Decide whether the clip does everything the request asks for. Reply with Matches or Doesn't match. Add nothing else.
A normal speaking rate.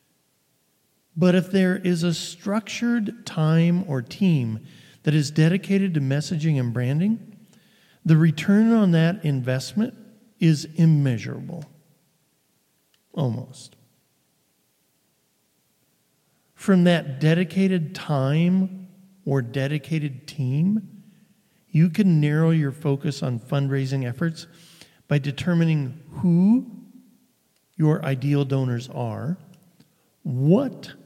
Doesn't match